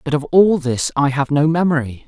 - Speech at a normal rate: No, fast, 230 wpm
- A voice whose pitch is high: No, medium, 150 Hz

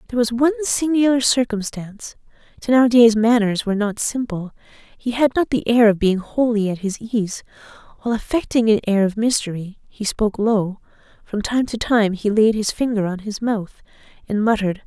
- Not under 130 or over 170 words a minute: No, average, 180 wpm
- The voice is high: Yes, high, 225 Hz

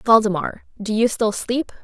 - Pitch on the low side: No, high, 220 Hz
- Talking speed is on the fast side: No, average, 165 wpm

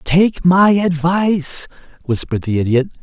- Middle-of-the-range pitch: Yes, medium, 165 Hz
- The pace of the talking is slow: Yes, slow, 120 wpm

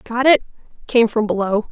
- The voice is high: Yes, high, 230 Hz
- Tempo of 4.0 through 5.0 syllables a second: Yes, 4.8 syllables/s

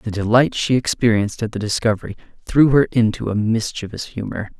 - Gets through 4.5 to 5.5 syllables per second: No, 5.8 syllables/s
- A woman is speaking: No, male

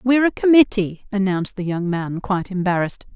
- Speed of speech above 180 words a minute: No, average, 170 wpm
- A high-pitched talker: Yes, high, 200 Hz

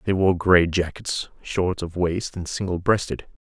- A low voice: Yes, very low, 90 Hz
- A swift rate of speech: No, average, 175 wpm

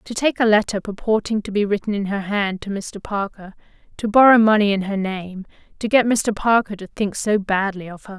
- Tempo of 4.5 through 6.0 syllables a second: Yes, 5.3 syllables/s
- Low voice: No, high, 205 Hz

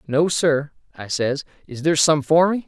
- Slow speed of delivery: No, average, 200 wpm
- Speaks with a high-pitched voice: No, medium, 155 Hz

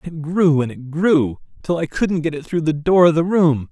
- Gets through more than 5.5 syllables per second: No, 4.7 syllables/s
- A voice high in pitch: No, medium, 155 Hz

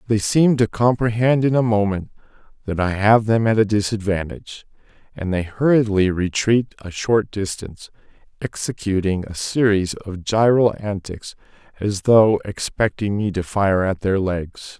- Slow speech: No, average, 145 wpm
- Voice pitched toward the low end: Yes, low, 105 Hz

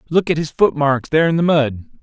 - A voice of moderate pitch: Yes, medium, 150 Hz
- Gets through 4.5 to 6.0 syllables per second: No, 6.2 syllables/s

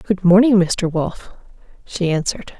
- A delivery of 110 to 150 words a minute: Yes, average, 140 wpm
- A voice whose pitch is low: No, medium, 185 Hz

